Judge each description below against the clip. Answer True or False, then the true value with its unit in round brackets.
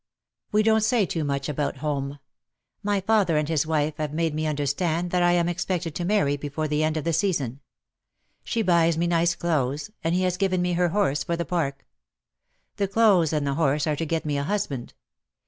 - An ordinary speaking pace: False (210 wpm)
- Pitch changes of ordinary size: True (3.4 semitones)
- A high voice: False (165 Hz)